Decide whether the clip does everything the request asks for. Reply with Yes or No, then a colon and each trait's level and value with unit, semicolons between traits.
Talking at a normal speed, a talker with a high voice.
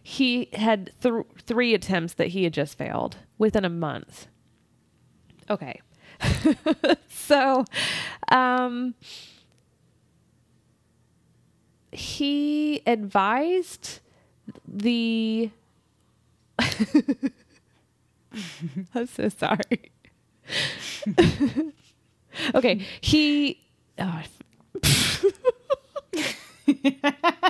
No: slow, 55 wpm; very high, 250 Hz